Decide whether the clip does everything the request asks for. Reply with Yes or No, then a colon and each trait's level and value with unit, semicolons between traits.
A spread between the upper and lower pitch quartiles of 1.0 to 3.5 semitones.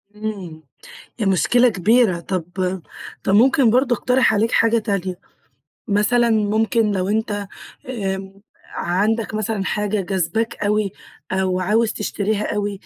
Yes: average, 2.7 semitones